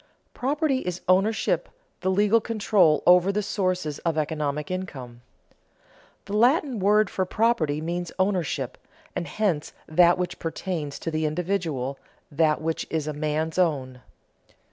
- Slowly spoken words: Yes, slow, 130 wpm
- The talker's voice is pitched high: No, medium, 175 Hz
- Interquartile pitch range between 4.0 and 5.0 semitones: Yes, average, 4.7 semitones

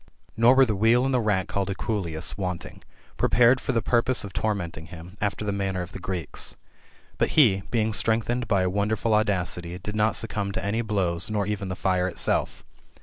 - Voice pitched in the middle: No, low, 100 Hz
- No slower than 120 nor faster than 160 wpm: No, average, 195 wpm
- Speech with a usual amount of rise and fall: Yes, average, 3.3 semitones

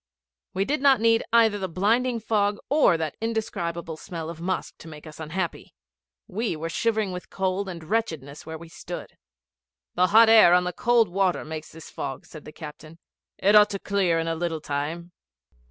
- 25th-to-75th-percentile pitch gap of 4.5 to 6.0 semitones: Yes, average, 4.9 semitones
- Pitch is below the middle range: No, medium, 180 Hz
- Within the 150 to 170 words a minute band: No, average, 185 wpm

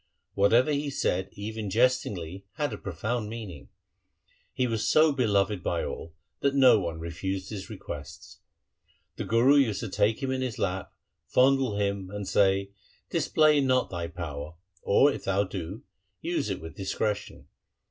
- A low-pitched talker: Yes, low, 105 Hz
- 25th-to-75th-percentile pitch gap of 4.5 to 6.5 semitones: Yes, average, 5.2 semitones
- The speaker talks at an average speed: Yes, average, 160 wpm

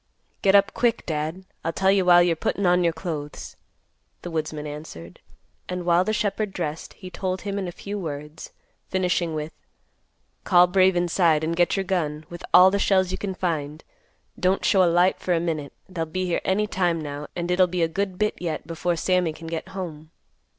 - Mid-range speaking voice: Yes, medium, 175 Hz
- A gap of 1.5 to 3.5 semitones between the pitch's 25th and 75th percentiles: Yes, average, 2.8 semitones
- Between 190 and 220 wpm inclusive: Yes, average, 200 wpm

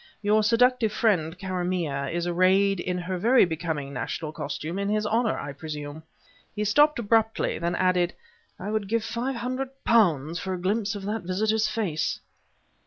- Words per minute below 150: No, average, 165 wpm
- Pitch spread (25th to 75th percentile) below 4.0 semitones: No, average, 4.4 semitones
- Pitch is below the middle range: No, high, 195 Hz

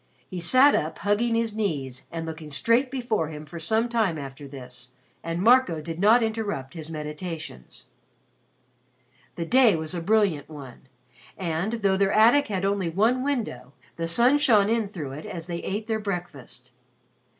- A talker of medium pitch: Yes, medium, 180 Hz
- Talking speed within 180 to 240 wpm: No, average, 165 wpm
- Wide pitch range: Yes, wide, 6.1 semitones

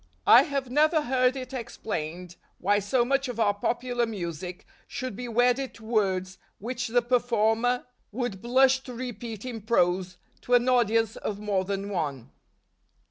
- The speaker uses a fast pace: No, average, 155 wpm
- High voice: Yes, high, 230 Hz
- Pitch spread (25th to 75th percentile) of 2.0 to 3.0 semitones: No, average, 3.9 semitones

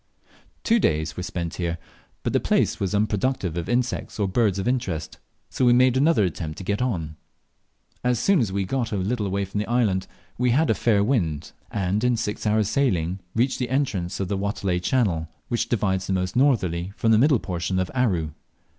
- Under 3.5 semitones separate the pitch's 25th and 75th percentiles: No, average, 5.2 semitones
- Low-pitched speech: Yes, low, 100 Hz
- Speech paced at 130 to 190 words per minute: No, average, 200 wpm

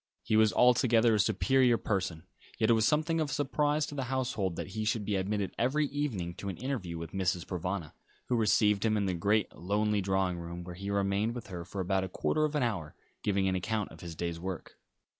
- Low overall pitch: Yes, low, 100 Hz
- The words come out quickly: Yes, fast, 225 wpm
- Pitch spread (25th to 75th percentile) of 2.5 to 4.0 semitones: No, average, 4.5 semitones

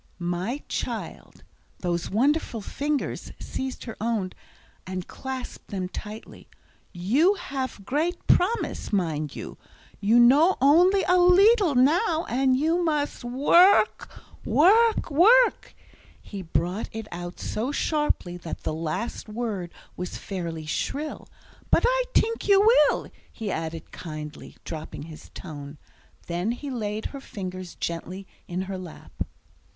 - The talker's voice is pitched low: No, high, 230 Hz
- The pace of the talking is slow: Yes, slow, 125 wpm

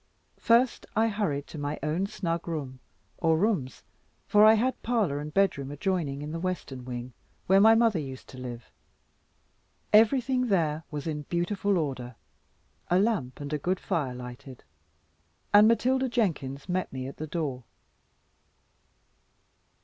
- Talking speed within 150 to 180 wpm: No, average, 140 wpm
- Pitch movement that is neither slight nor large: No, wide, 6.9 semitones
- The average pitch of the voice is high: No, medium, 165 Hz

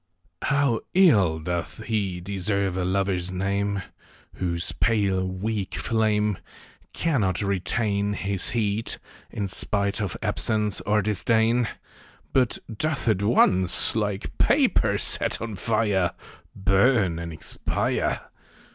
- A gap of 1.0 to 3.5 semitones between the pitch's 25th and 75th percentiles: Yes, average, 2.9 semitones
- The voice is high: No, low, 100 Hz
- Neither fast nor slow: No, slow, 110 wpm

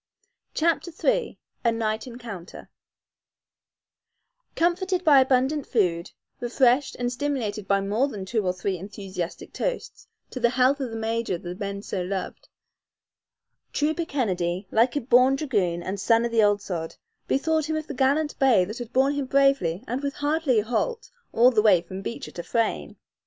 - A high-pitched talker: Yes, high, 235 Hz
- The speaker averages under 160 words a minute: No, average, 170 wpm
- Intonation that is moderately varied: No, wide, 5.8 semitones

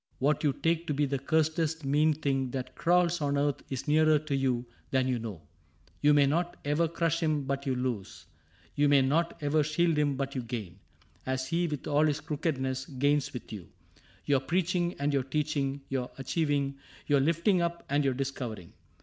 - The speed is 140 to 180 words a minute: No, average, 195 wpm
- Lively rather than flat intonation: No, average, 2.8 semitones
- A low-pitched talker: No, medium, 145 Hz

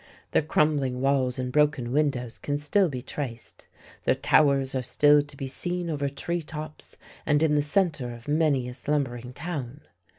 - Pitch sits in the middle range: Yes, medium, 145 Hz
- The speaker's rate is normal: Yes, average, 170 wpm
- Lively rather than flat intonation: No, average, 2.8 semitones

